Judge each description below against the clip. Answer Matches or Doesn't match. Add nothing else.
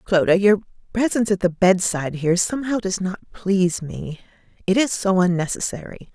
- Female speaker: Matches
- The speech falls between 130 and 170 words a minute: Matches